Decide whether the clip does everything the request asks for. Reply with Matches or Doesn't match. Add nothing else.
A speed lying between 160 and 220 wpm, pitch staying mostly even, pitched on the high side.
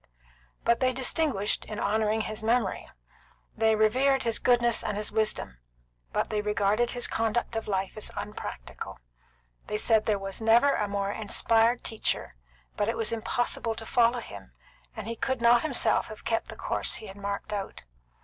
Matches